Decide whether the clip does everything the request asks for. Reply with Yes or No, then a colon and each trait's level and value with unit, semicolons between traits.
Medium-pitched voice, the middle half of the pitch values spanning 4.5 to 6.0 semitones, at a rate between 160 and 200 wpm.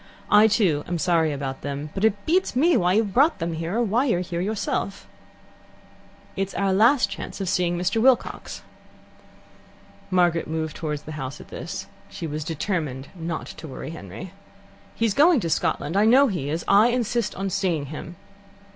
Yes: medium, 180 Hz; wide, 5.5 semitones; average, 175 wpm